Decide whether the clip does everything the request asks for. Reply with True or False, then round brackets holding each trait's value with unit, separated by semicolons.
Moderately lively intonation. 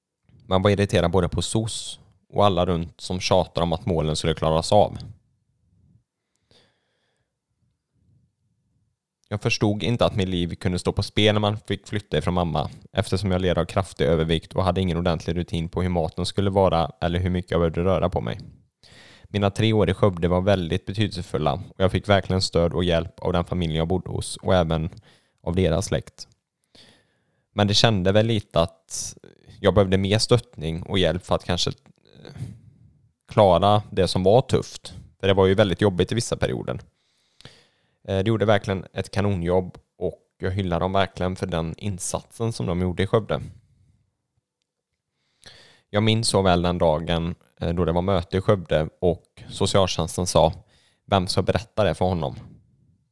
True (3.0 semitones)